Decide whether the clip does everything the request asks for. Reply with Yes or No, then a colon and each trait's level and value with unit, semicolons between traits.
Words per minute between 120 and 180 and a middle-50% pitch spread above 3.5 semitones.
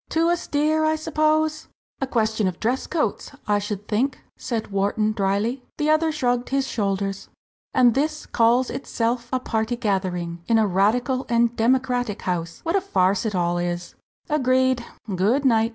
Yes: average, 160 wpm; average, 4.9 semitones